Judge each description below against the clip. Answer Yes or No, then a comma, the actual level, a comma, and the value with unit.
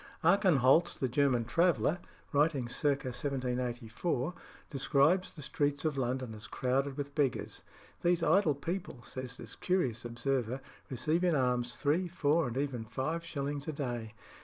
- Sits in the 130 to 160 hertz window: Yes, medium, 140 Hz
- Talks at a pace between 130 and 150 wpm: Yes, average, 140 wpm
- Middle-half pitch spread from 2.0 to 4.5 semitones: Yes, average, 4.0 semitones